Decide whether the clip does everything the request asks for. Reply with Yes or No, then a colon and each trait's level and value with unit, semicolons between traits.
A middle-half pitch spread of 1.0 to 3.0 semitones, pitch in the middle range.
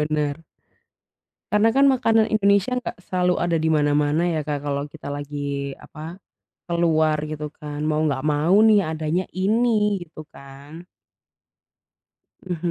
No: average, 4.2 semitones; medium, 160 Hz